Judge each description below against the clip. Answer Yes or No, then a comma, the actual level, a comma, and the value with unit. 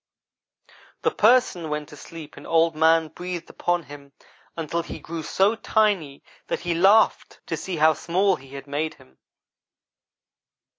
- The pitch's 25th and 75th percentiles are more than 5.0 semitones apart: No, average, 3.1 semitones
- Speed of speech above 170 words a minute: No, average, 150 wpm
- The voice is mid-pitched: Yes, medium, 165 Hz